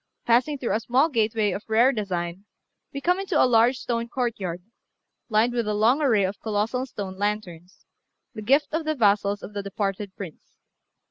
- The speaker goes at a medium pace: Yes, average, 180 wpm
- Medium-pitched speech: No, high, 215 Hz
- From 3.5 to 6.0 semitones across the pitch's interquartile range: Yes, average, 3.8 semitones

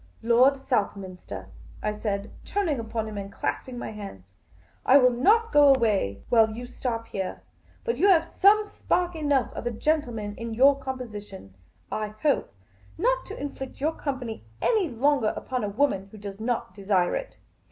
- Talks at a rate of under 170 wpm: No, average, 175 wpm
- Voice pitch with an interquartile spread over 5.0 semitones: Yes, wide, 5.5 semitones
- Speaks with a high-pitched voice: Yes, high, 235 Hz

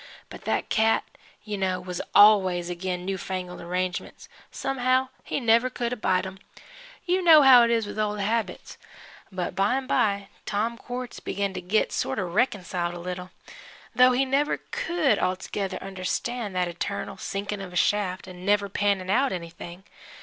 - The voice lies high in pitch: Yes, high, 200 Hz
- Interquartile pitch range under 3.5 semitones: No, average, 4.5 semitones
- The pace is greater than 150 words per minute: Yes, average, 165 wpm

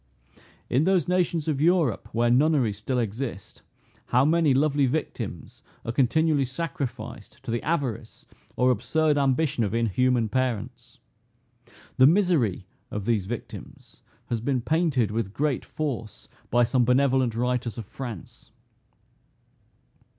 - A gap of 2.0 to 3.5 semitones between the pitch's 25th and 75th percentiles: No, average, 4.5 semitones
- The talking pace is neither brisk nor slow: No, slow, 125 wpm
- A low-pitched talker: Yes, low, 130 Hz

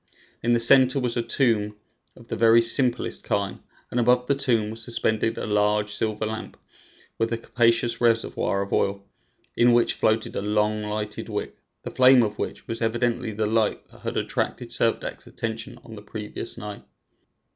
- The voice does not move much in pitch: Yes, narrow, 2.1 semitones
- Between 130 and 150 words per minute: No, average, 175 wpm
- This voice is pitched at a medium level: No, low, 115 Hz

